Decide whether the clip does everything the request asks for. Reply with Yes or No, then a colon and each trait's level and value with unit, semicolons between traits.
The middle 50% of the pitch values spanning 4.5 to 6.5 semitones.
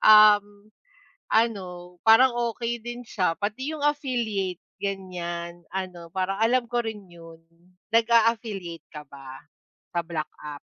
Yes: average, 4.8 semitones